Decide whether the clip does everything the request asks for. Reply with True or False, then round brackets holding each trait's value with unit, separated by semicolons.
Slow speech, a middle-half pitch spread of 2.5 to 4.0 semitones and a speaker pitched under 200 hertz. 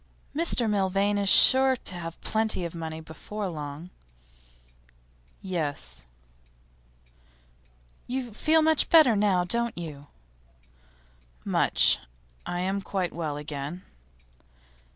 False (100 wpm; 5.3 semitones; 185 Hz)